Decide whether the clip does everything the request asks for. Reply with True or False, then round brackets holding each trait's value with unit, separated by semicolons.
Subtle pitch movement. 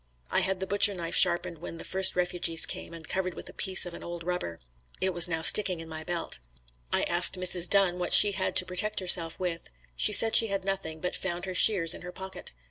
True (2.0 semitones)